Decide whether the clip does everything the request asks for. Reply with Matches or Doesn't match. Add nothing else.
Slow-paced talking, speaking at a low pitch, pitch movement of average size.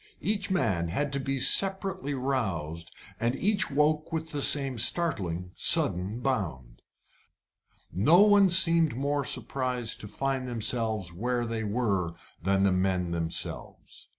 Doesn't match